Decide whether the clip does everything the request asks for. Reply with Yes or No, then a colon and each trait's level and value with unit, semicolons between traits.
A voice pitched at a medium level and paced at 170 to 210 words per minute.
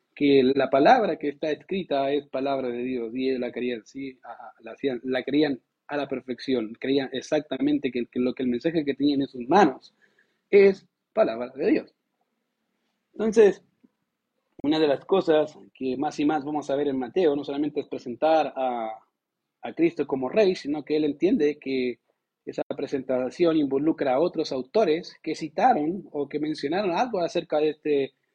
Yes: medium, 145 Hz; average, 175 wpm